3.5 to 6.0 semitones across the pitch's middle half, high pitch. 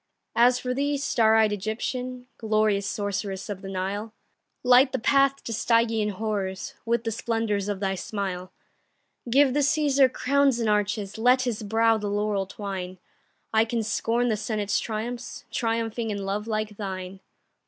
No: average, 2.9 semitones; high, 220 Hz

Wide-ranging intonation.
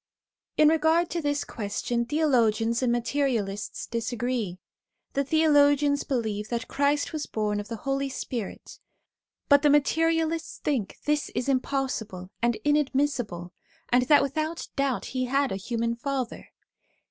No: average, 3.9 semitones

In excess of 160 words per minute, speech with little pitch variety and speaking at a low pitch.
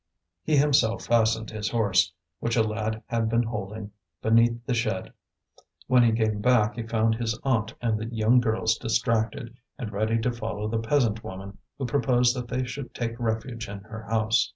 Yes: average, 180 wpm; narrow, 1.5 semitones; low, 115 Hz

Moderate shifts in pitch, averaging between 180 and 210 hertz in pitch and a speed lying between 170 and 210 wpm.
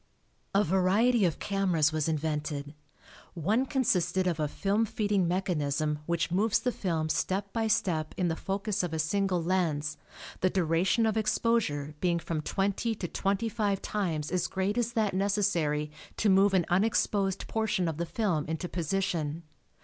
No: average, 4.1 semitones; medium, 185 Hz; average, 160 wpm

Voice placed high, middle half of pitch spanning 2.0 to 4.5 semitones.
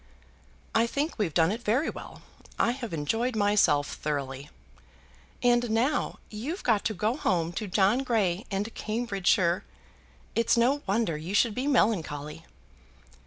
No: high, 215 Hz; wide, 5.6 semitones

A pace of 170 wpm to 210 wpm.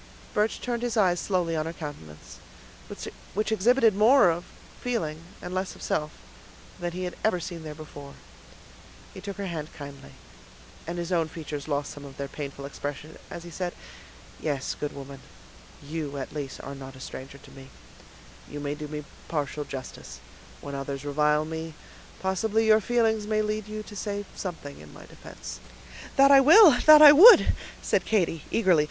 Yes: average, 175 wpm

